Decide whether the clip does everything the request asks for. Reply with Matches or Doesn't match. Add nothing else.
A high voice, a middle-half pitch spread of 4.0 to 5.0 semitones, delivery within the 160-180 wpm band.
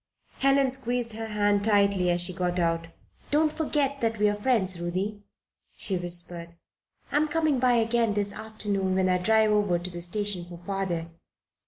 Matches